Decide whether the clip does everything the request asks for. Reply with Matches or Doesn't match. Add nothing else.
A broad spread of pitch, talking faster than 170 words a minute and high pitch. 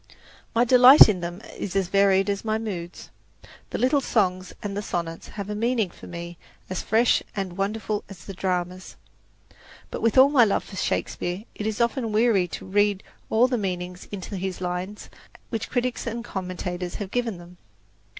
Doesn't match